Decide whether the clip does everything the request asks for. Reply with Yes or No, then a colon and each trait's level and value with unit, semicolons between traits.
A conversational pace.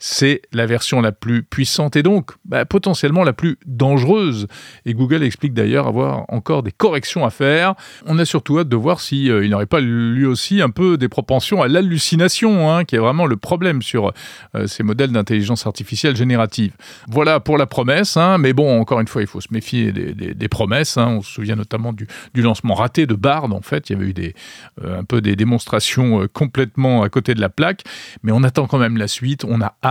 No: fast, 225 wpm